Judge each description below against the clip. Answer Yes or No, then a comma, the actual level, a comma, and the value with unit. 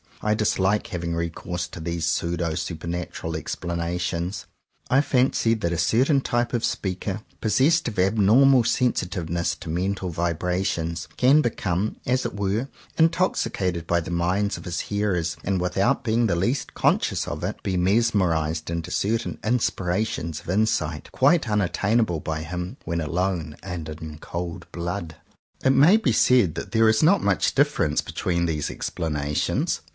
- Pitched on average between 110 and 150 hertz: No, very low, 90 Hz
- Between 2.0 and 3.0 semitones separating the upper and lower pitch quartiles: No, average, 4.9 semitones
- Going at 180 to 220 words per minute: No, average, 155 wpm